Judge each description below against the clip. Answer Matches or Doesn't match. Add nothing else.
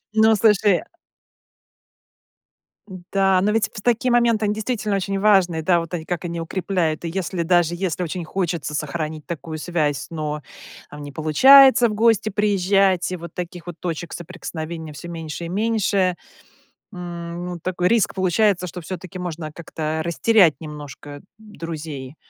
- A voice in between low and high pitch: Matches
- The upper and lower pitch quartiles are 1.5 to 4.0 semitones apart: Matches